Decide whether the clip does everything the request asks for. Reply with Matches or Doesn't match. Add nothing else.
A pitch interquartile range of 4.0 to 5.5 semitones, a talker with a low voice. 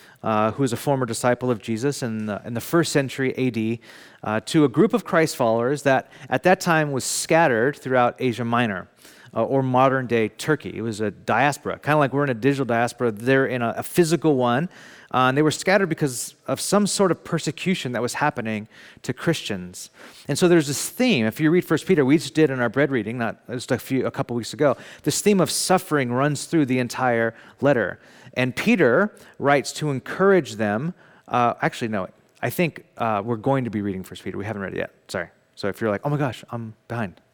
Matches